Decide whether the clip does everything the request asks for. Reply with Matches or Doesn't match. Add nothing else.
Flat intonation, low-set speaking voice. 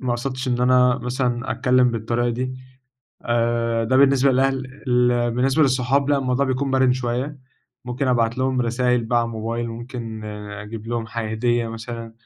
Matches